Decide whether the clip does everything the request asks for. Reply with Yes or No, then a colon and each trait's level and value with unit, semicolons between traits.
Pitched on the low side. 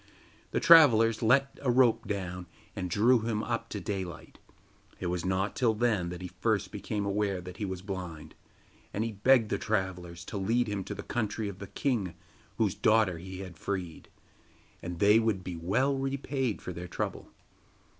Yes: low, 100 Hz